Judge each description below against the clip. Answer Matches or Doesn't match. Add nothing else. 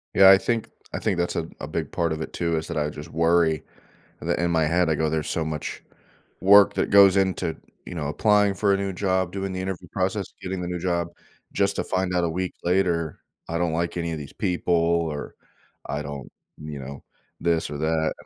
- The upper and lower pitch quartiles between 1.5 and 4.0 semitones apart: Matches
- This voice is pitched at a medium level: Doesn't match